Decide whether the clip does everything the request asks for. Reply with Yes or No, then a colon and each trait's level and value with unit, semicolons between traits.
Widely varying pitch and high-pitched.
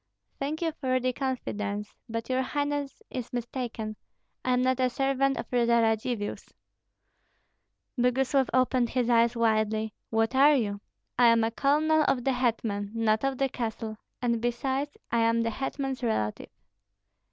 No: average, 3.0 semitones; high, 245 Hz